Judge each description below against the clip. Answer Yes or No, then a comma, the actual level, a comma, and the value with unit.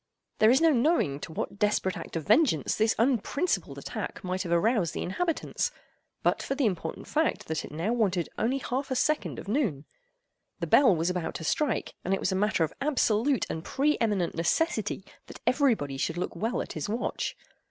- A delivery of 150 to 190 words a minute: No, average, 200 wpm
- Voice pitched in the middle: No, high, 215 Hz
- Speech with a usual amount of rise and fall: No, wide, 7.5 semitones